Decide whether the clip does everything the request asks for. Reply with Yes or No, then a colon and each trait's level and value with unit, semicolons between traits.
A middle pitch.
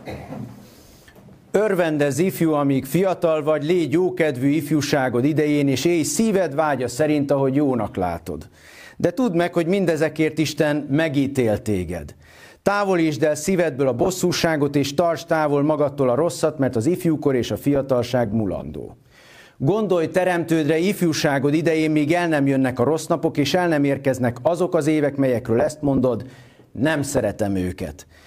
Yes: medium, 150 Hz